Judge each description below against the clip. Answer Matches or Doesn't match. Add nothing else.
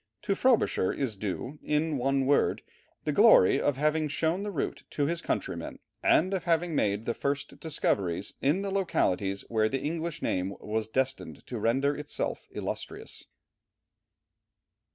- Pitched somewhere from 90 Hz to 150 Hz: Matches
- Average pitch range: Doesn't match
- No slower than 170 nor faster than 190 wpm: Doesn't match